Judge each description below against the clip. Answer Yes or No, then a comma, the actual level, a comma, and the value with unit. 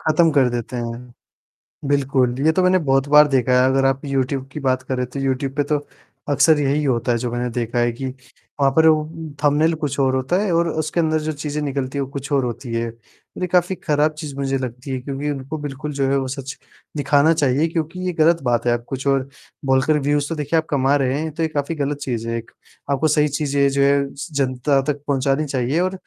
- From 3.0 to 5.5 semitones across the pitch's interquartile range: No, narrow, 2.6 semitones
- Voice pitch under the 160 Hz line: Yes, medium, 140 Hz